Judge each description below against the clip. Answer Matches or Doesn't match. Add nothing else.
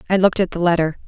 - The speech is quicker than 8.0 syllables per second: Matches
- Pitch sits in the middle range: Matches